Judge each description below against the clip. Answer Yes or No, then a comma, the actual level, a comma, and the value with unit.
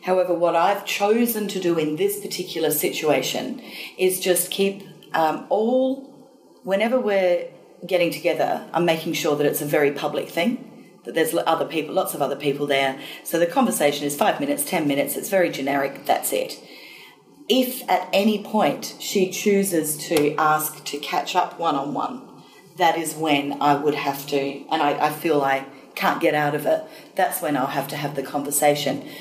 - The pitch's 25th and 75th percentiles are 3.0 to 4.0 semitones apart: No, average, 5.2 semitones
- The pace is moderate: Yes, average, 185 wpm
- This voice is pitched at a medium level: Yes, medium, 165 Hz